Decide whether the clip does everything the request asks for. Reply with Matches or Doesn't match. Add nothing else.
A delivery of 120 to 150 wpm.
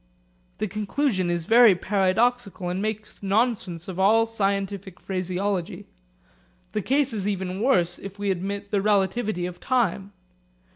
Matches